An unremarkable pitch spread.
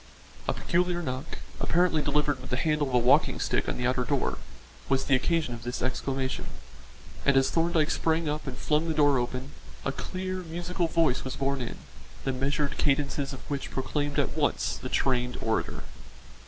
Yes: average, 3.6 semitones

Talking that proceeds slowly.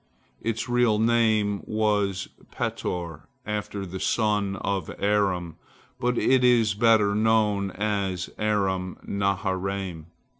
Yes: slow, 105 wpm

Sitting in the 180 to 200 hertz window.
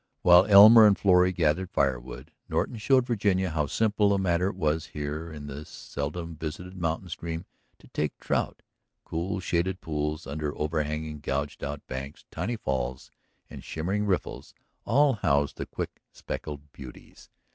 No: very low, 80 Hz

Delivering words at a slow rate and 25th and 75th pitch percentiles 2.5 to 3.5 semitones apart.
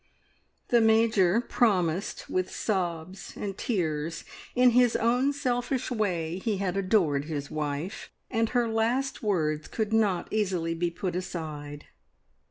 No: slow, 130 wpm; wide, 5.4 semitones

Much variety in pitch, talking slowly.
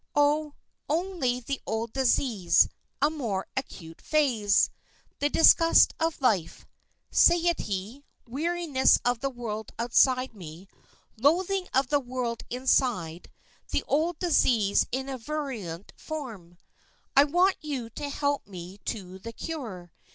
Yes: wide, 5.9 semitones; slow, 125 wpm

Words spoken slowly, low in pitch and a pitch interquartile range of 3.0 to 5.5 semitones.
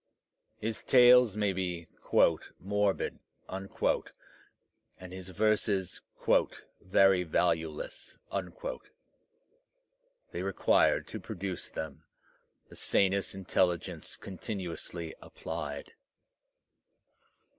No: slow, 70 wpm; very low, 95 Hz; narrow, 2.6 semitones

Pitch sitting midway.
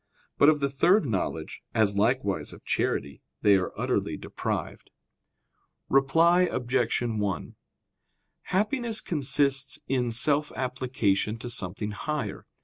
No: low, 130 Hz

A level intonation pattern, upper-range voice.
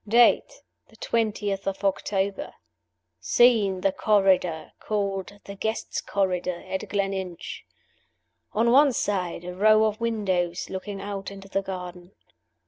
Yes: narrow, 2.2 semitones; high, 195 Hz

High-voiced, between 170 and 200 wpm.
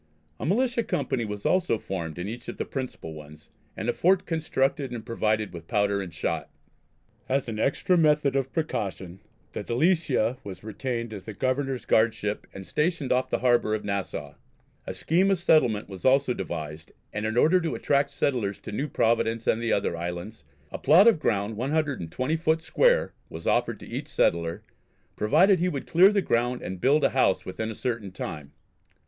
No: low, 120 Hz; average, 185 wpm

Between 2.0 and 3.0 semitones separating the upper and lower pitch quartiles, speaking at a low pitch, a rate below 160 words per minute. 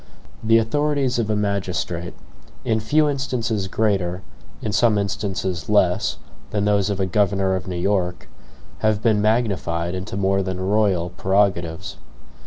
Yes: average, 2.7 semitones; low, 100 Hz; average, 140 wpm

